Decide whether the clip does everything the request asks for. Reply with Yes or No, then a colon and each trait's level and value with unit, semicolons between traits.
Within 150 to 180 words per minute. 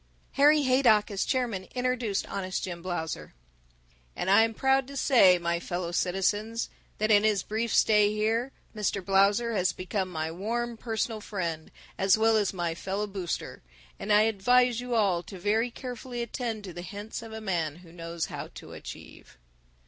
Yes: average, 170 wpm